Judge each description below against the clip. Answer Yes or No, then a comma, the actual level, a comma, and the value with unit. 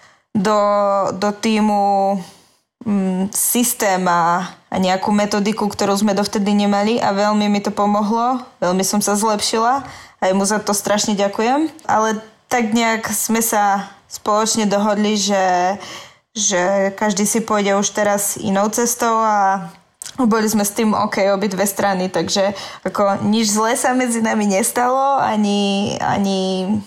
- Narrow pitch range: Yes, narrow, 1.8 semitones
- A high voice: Yes, high, 205 Hz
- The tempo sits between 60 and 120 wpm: No, average, 140 wpm